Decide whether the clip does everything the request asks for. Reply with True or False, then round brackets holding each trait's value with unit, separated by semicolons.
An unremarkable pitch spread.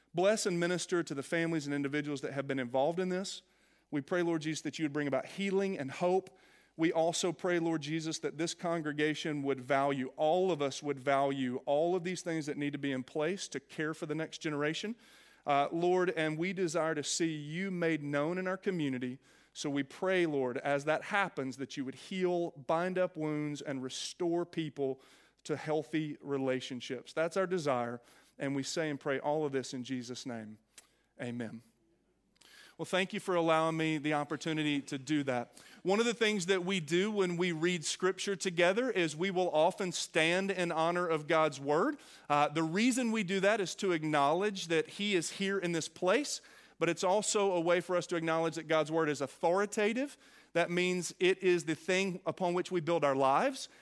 True (4.1 semitones)